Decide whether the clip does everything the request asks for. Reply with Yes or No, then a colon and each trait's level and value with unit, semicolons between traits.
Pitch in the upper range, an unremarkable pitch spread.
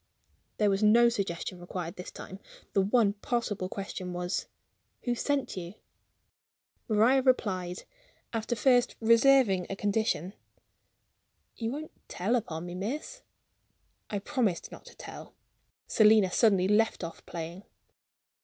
Yes: high, 205 Hz; average, 4.5 semitones